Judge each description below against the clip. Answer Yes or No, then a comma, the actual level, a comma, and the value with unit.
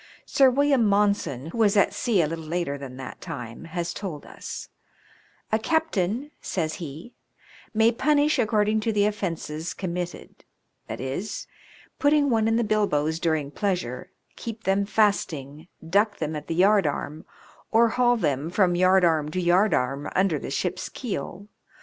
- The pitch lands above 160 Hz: Yes, medium, 185 Hz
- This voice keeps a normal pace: Yes, average, 150 wpm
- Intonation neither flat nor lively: No, wide, 5.7 semitones